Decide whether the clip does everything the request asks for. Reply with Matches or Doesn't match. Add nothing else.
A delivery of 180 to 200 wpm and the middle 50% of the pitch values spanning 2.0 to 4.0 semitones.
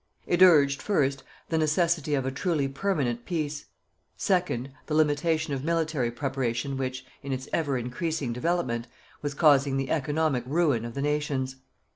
Doesn't match